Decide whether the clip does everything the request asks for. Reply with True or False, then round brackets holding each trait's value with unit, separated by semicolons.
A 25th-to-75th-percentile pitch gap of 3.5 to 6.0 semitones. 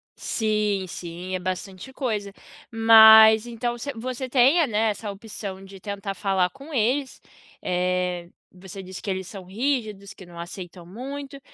True (4.3 semitones)